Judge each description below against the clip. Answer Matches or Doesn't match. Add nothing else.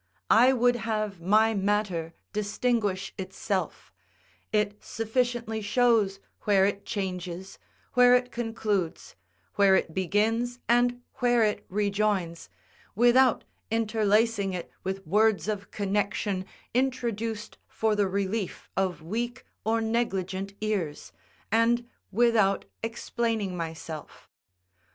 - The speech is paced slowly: Matches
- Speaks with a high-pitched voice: Matches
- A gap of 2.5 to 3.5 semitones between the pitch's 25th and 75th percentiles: Matches